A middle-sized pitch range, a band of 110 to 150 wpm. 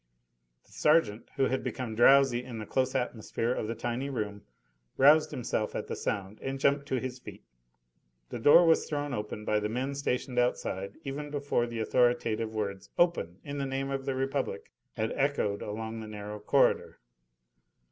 No: average, 4.1 semitones; average, 175 wpm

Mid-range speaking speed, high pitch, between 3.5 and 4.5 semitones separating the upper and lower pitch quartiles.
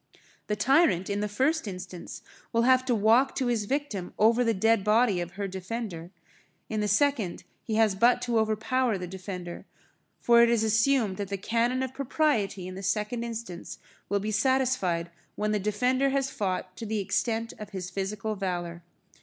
Yes: average, 180 wpm; high, 215 Hz; average, 3.9 semitones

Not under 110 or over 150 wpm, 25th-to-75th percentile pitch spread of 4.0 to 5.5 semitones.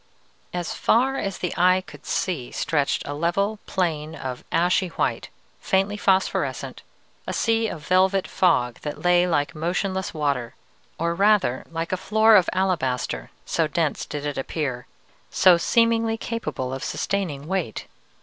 Yes: average, 145 wpm; average, 4.8 semitones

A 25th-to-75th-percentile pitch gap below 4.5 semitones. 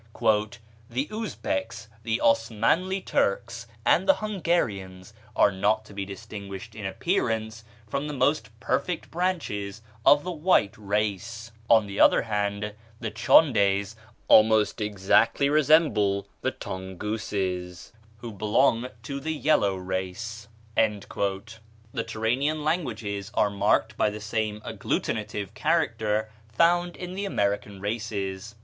No: average, 5.1 semitones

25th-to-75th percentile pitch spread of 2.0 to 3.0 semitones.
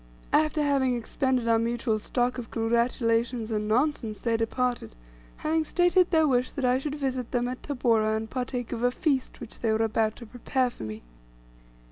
Yes: average, 2.7 semitones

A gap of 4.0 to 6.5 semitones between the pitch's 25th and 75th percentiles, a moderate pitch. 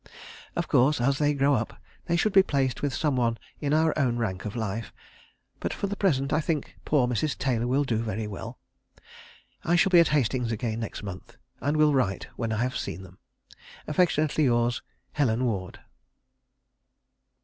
No: average, 4.7 semitones; low, 130 Hz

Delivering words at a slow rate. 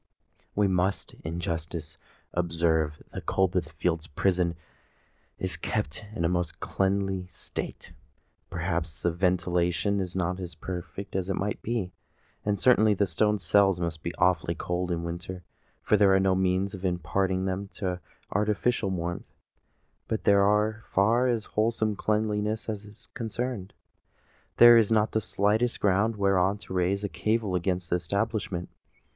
No: average, 150 wpm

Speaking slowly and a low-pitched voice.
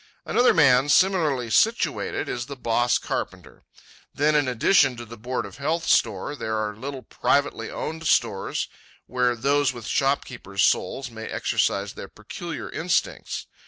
No: average, 145 wpm; low, 125 Hz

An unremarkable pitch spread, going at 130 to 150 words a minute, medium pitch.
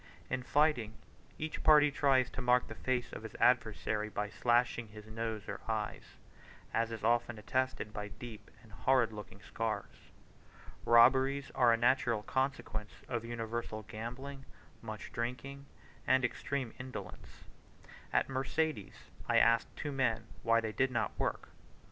No: average, 3.1 semitones; average, 140 wpm; low, 120 Hz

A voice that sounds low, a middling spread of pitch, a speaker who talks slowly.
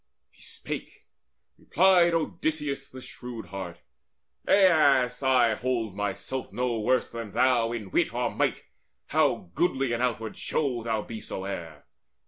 Yes: low, 125 Hz; average, 3.6 semitones; slow, 130 wpm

